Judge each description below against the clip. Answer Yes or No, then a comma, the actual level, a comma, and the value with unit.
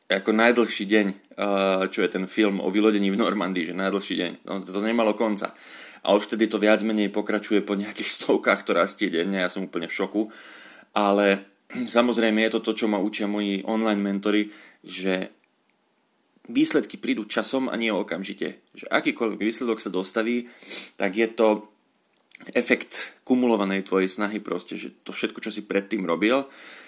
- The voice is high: No, low, 105 Hz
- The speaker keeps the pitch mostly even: Yes, narrow, 2.2 semitones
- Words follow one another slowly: No, fast, 165 wpm